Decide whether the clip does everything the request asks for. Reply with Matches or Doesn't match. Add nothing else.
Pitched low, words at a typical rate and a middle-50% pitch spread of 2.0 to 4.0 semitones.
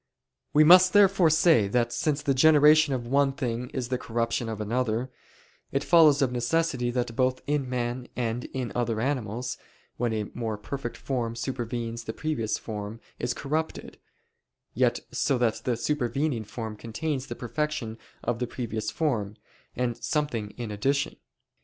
Matches